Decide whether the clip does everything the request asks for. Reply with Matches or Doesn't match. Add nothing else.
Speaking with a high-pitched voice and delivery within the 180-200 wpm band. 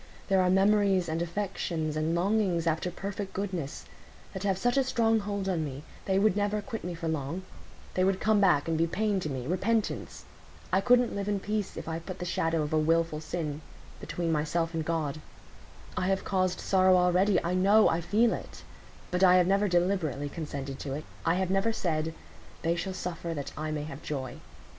Doesn't match